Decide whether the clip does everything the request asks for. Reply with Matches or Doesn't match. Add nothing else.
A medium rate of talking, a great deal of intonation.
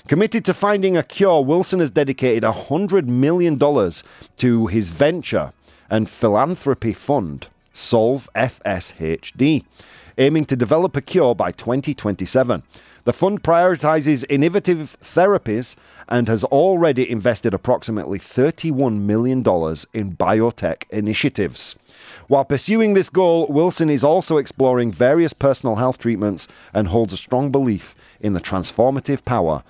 Doesn't match